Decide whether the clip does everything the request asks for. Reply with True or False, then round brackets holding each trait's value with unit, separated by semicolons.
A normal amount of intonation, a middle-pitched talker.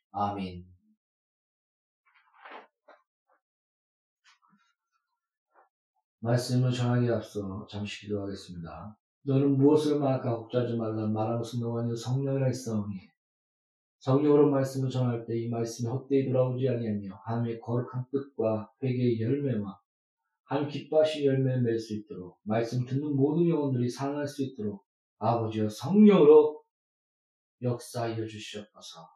False (4.0 semitones; 120 Hz)